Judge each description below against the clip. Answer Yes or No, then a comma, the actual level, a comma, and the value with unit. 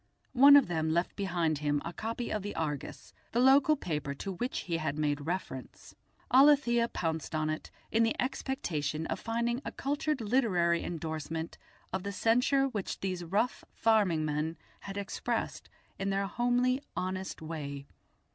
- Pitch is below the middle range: No, high, 190 Hz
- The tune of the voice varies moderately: No, wide, 7.0 semitones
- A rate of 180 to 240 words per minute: No, average, 155 wpm